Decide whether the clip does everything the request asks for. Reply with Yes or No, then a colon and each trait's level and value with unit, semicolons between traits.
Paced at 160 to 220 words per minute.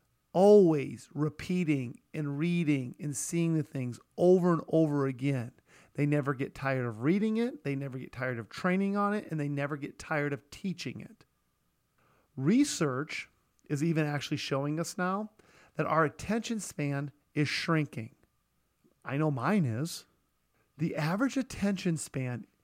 No: average, 150 wpm